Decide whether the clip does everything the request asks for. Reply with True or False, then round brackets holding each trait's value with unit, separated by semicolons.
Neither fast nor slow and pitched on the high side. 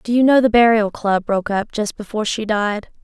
False (240 wpm; 215 Hz)